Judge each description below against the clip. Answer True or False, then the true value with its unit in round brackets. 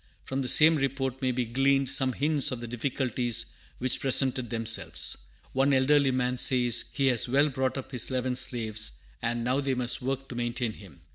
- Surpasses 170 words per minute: True (190 wpm)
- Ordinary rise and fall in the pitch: False (2.1 semitones)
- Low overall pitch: True (130 Hz)